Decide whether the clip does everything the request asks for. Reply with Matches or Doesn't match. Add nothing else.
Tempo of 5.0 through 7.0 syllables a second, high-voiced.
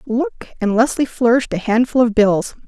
Matches